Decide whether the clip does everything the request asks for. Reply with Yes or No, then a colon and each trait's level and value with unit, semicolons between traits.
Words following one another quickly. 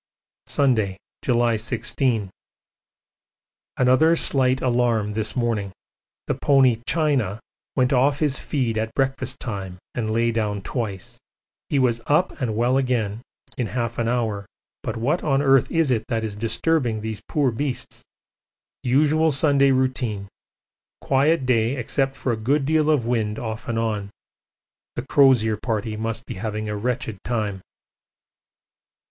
No: average, 140 wpm